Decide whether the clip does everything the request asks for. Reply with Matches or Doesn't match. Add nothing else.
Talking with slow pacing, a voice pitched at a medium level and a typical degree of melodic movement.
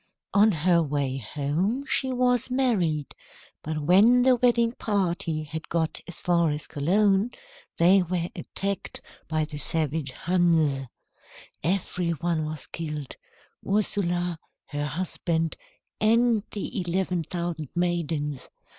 Matches